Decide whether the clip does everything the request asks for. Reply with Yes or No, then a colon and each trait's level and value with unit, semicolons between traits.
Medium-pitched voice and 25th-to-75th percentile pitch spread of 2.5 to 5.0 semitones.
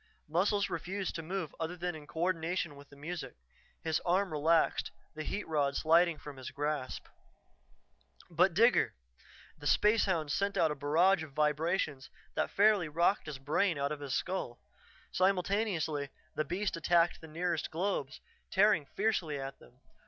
Yes: medium, 165 Hz; average, 3.8 semitones